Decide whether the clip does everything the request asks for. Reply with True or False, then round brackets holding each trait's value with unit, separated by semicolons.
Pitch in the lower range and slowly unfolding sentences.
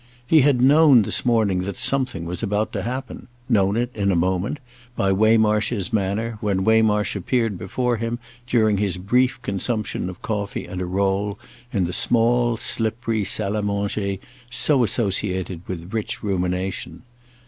False (105 Hz; 150 wpm)